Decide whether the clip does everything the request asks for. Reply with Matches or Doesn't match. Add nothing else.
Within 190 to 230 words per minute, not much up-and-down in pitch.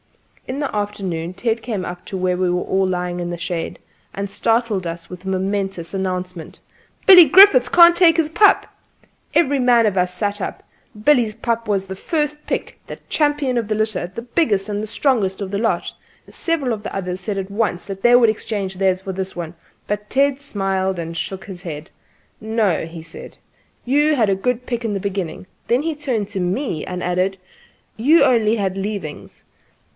Doesn't match